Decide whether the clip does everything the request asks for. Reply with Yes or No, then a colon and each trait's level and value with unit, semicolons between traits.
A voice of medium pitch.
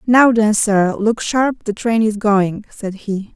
No: high, 215 Hz